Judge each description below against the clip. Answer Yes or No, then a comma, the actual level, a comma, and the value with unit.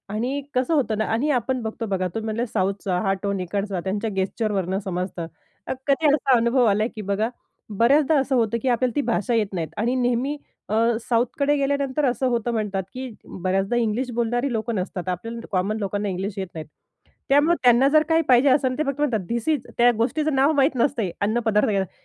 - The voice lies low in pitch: No, high, 230 Hz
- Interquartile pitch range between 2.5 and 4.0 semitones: No, average, 4.5 semitones